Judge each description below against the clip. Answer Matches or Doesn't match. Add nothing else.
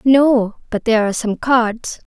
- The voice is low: Doesn't match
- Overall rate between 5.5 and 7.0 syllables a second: Doesn't match